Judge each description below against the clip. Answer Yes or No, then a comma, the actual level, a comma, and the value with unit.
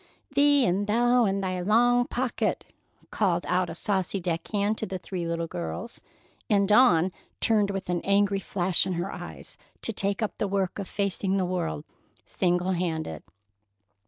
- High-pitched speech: Yes, high, 195 Hz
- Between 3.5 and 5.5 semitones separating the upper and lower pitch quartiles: No, average, 2.8 semitones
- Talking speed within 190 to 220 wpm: No, average, 165 wpm